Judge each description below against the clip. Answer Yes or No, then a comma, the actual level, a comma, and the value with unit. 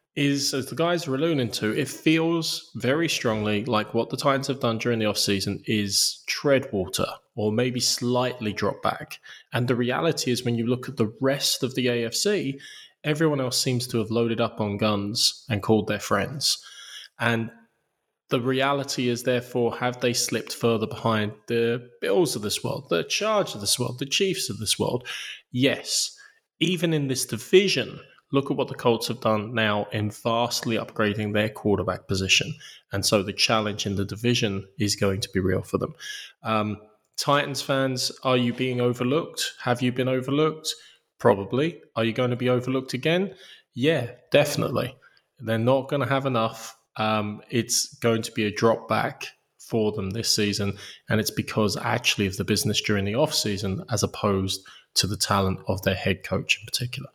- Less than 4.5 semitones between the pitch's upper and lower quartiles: Yes, average, 4.0 semitones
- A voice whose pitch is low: Yes, low, 120 Hz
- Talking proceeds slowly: No, average, 180 wpm